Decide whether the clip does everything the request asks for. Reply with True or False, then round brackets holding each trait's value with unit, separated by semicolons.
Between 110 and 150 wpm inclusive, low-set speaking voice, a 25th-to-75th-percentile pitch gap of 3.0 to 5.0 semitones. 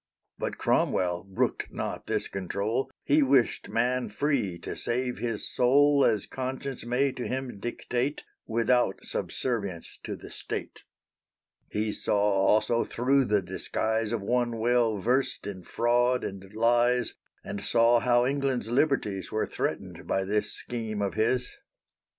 True (140 wpm; 120 Hz; 3.3 semitones)